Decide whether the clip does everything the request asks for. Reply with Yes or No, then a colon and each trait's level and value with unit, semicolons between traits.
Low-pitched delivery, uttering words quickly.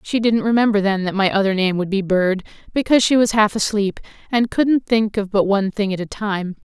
No: high, 205 Hz; fast, 230 wpm